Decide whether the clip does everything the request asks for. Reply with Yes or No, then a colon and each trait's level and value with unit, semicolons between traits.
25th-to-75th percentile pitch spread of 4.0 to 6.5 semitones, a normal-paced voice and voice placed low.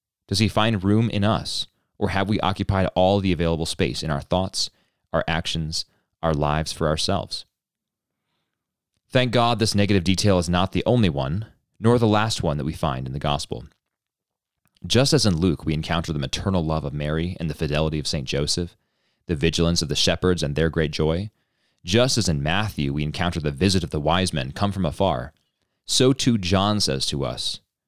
Yes: average, 4.3 semitones; average, 195 wpm; very low, 90 Hz